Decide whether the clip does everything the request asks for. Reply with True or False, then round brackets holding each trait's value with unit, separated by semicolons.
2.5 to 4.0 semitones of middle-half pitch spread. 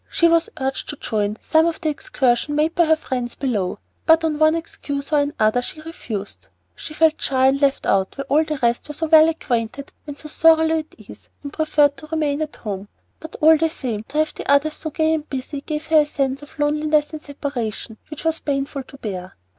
True (3.0 semitones)